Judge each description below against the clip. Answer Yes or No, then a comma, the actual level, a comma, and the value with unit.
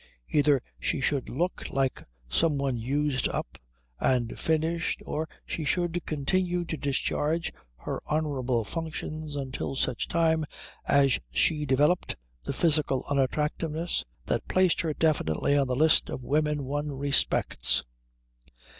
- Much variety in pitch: No, average, 3.0 semitones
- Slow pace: Yes, slow, 130 wpm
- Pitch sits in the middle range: Yes, medium, 150 Hz